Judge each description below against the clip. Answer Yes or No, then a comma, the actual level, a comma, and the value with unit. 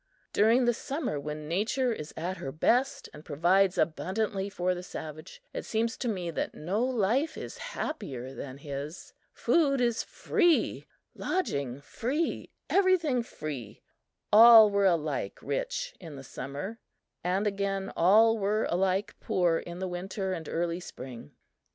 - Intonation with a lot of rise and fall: Yes, wide, 6.6 semitones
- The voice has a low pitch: No, high, 190 Hz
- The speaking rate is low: No, average, 145 wpm